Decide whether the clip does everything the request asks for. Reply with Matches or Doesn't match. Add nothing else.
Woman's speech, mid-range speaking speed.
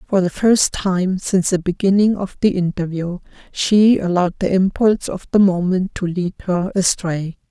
Matches